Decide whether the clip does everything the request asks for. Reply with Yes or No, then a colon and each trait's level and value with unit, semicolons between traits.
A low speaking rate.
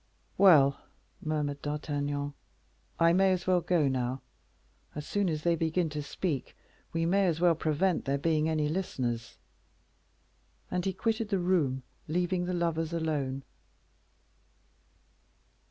Yes: slow, 130 wpm